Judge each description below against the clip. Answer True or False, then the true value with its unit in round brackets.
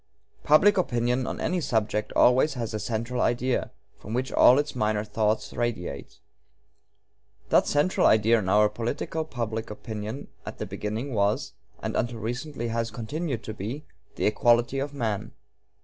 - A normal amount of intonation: True (3.4 semitones)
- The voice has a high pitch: False (115 Hz)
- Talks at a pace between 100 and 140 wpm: False (150 wpm)